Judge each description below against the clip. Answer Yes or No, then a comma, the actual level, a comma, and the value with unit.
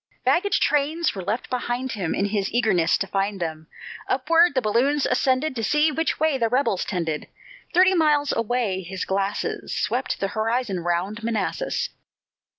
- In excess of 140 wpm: Yes, average, 155 wpm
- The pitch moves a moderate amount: No, wide, 6.6 semitones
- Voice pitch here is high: Yes, high, 230 Hz